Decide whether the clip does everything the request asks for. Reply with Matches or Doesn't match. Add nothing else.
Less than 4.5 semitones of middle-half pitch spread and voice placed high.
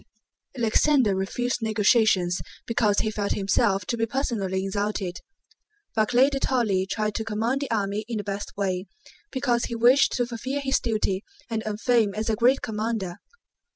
Matches